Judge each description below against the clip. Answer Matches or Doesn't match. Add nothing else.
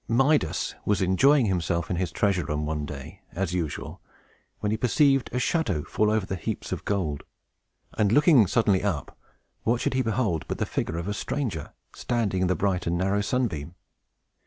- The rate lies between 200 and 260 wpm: Doesn't match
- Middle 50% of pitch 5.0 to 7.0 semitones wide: Matches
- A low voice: Matches